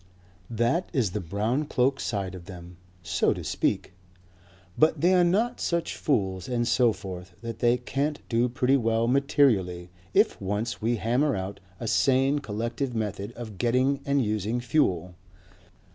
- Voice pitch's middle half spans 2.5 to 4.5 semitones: No, average, 5.2 semitones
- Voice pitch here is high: No, low, 120 Hz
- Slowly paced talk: No, average, 155 wpm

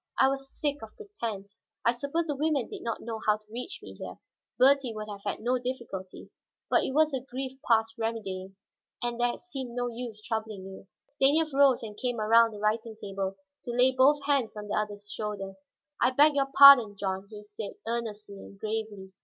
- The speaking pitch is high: Yes, high, 230 Hz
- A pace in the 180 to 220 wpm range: Yes, average, 195 wpm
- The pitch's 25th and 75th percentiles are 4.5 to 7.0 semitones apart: No, average, 4.1 semitones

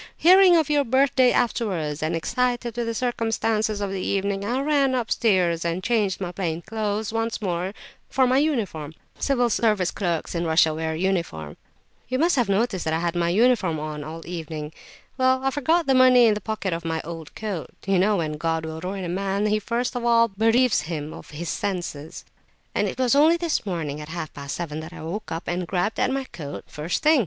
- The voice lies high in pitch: Yes, high, 195 Hz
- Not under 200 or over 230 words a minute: Yes, fast, 205 wpm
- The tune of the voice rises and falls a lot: Yes, wide, 6.5 semitones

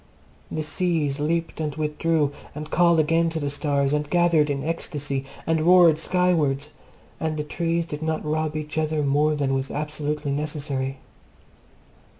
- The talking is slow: No, average, 155 wpm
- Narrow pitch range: Yes, narrow, 2.0 semitones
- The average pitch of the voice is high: No, medium, 150 Hz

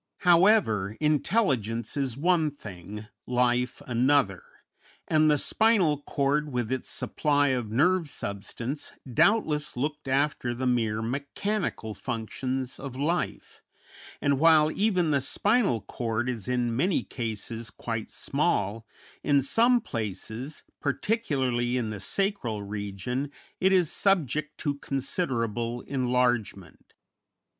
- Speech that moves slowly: Yes, slow, 115 wpm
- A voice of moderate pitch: No, low, 130 Hz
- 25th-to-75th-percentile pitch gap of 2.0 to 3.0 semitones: No, average, 4.8 semitones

